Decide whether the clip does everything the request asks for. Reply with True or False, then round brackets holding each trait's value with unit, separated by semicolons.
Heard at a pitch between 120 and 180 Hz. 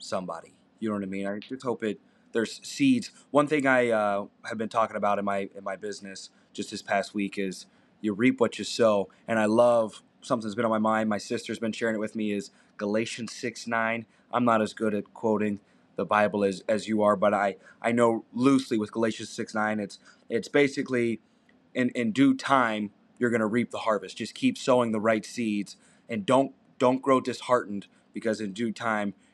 False (110 Hz)